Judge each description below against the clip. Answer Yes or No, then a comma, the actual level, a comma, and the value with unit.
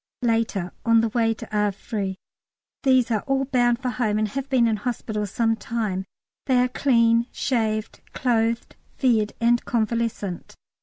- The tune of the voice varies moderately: No, narrow, 2.3 semitones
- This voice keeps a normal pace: Yes, average, 145 wpm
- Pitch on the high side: Yes, high, 230 Hz